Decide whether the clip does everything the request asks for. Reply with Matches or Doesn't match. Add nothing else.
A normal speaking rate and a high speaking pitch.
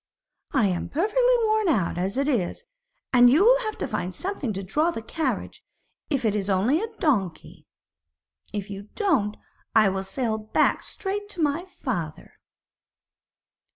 Matches